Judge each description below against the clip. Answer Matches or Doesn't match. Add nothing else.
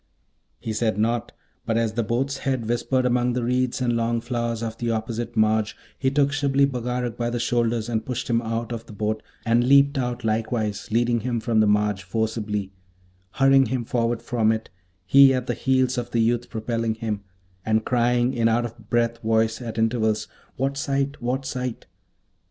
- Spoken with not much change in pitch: Matches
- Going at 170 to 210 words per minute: Matches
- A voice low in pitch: Matches